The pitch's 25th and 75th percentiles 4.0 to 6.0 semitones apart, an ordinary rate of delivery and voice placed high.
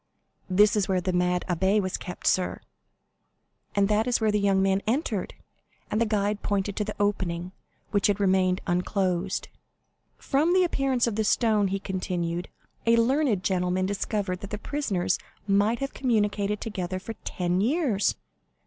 No: average, 2.9 semitones; average, 160 wpm; high, 200 Hz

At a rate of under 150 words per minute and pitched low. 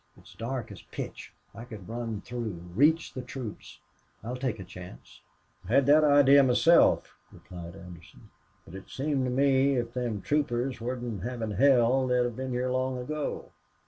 No: average, 165 wpm; low, 125 Hz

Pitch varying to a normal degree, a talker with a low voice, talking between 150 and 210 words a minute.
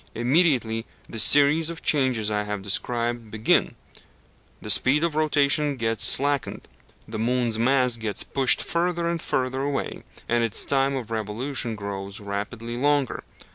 No: average, 4.3 semitones; low, 125 Hz; average, 140 wpm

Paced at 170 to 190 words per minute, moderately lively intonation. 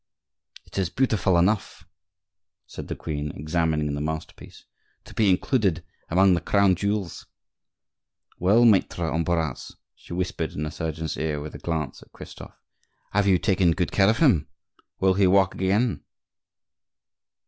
No: average, 145 wpm; average, 3.8 semitones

